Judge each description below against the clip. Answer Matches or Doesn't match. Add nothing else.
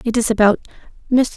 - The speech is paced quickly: Doesn't match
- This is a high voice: Matches